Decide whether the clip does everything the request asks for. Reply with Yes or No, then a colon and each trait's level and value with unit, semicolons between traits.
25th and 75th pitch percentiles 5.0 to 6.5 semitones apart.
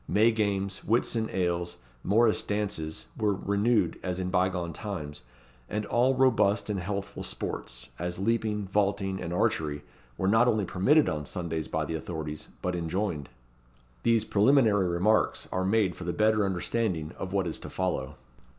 No: average, 3.6 semitones